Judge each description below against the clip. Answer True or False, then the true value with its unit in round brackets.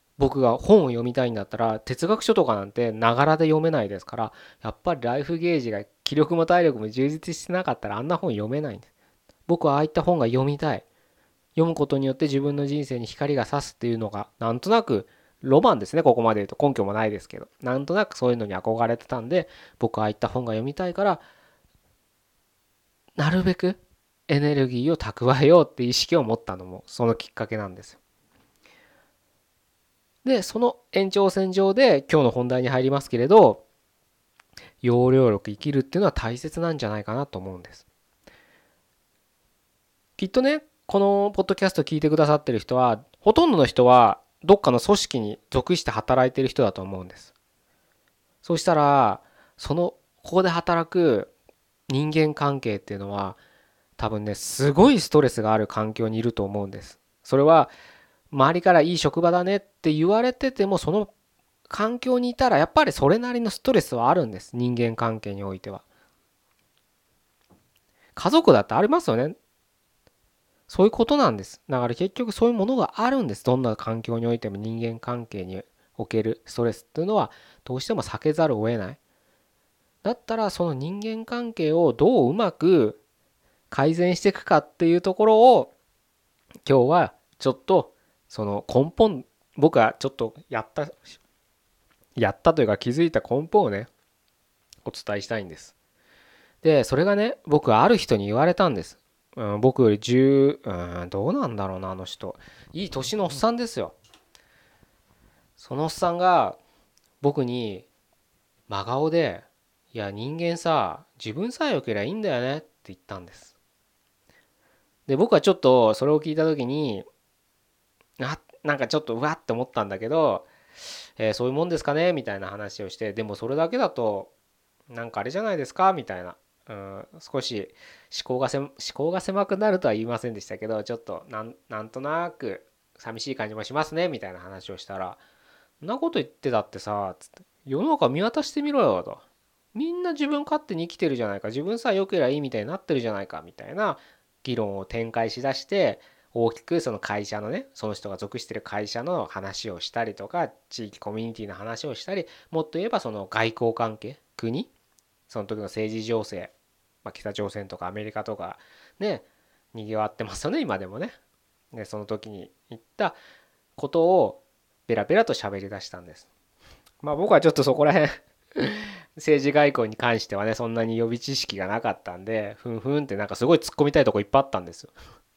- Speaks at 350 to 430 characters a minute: True (355 characters per minute)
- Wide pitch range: True (7.8 semitones)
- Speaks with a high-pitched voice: False (130 Hz)